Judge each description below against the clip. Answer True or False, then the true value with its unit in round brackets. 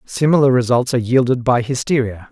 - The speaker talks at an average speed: True (155 wpm)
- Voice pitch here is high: False (125 Hz)